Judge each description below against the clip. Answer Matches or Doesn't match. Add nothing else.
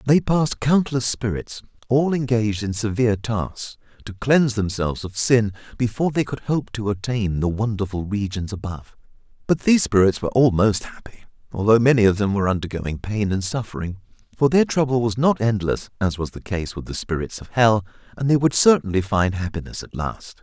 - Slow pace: Doesn't match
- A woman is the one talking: Doesn't match